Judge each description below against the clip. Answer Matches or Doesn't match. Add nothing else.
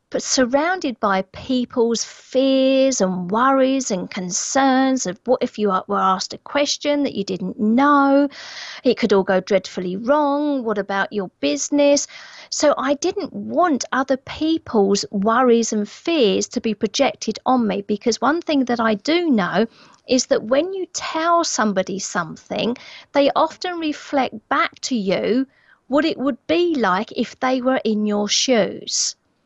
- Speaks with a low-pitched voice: Doesn't match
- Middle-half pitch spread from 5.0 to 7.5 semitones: Matches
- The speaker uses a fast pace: Doesn't match